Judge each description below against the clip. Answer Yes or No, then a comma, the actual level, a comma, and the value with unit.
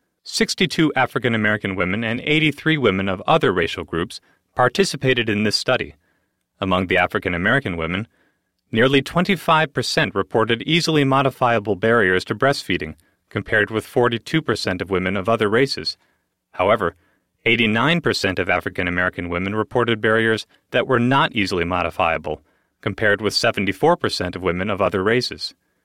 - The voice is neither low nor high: No, low, 115 Hz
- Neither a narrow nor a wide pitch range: No, wide, 5.8 semitones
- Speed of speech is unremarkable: No, slow, 130 wpm